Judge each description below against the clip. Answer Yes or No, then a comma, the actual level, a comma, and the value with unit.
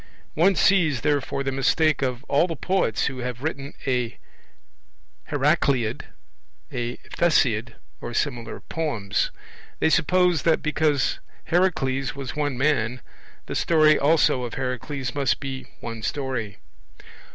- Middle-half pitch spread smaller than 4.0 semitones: Yes, average, 3.6 semitones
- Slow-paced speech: Yes, slow, 125 wpm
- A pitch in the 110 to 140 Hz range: Yes, low, 135 Hz